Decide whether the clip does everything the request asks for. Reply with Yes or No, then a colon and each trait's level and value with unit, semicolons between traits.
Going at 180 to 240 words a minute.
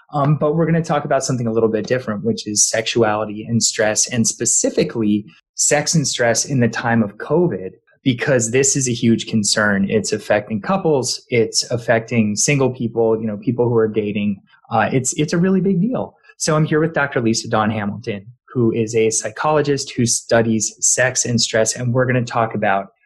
Yes: average, 200 wpm